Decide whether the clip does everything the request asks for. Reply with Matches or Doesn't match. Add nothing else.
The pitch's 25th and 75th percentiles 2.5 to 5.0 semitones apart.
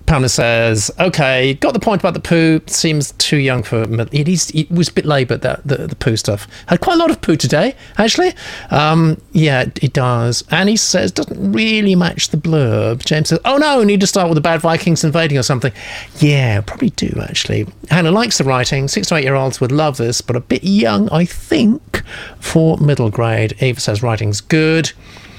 Doesn't match